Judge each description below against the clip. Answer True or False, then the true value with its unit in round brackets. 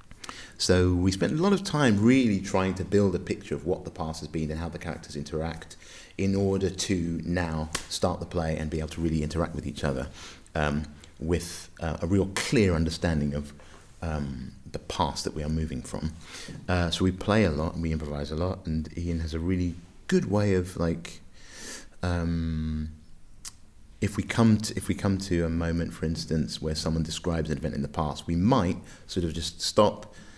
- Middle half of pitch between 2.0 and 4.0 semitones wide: True (3.0 semitones)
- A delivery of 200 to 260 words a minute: True (205 wpm)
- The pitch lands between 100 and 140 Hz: False (85 Hz)